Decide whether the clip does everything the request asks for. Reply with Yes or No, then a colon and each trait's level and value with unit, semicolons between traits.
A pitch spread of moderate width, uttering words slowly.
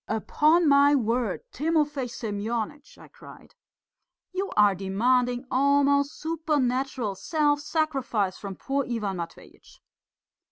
Yes: average, 5.0 semitones; slow, 105 wpm